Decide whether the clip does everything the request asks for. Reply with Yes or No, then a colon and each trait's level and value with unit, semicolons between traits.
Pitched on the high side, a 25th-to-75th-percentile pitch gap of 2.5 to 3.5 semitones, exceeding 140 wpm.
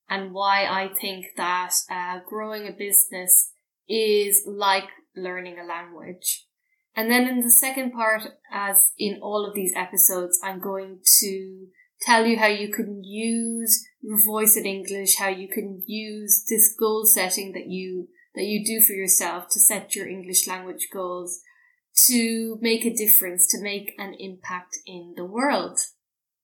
Yes: high, 200 Hz; average, 2.9 semitones; average, 160 wpm